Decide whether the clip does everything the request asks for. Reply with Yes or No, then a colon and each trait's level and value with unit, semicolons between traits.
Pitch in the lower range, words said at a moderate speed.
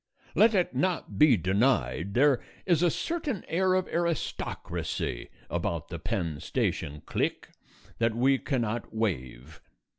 No: low, 125 Hz; slow, 125 wpm